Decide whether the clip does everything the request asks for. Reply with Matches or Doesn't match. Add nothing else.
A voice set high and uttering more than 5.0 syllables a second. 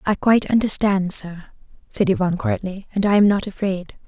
Matches